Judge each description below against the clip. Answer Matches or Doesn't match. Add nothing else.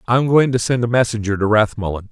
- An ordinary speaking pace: Doesn't match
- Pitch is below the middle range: Matches